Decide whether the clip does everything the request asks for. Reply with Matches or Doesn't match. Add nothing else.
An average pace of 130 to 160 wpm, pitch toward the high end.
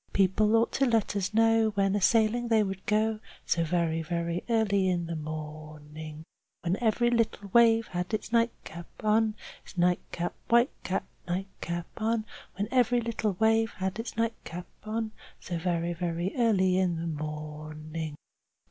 Matches